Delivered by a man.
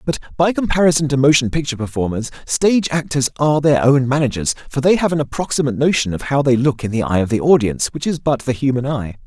Yes: male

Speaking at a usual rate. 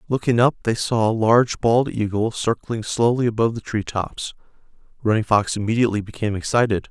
Yes: average, 165 wpm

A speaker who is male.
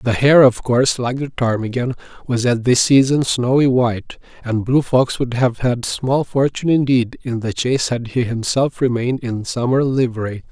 Yes: male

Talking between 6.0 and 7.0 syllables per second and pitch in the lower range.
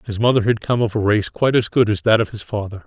Yes: 6.6 syllables/s; low, 110 Hz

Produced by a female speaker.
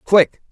No: male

